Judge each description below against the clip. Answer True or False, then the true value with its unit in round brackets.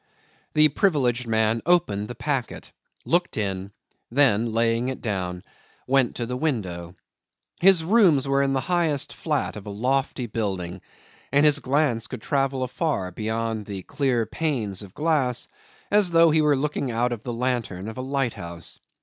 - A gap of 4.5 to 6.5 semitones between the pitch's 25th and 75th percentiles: True (5.0 semitones)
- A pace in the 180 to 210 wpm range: False (160 wpm)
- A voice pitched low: True (125 Hz)